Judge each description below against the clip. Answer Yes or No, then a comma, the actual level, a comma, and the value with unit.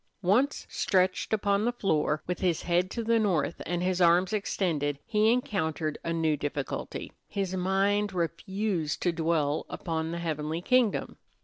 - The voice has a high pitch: No, medium, 180 Hz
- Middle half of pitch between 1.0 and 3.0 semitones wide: No, average, 3.9 semitones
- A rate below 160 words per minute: Yes, average, 150 wpm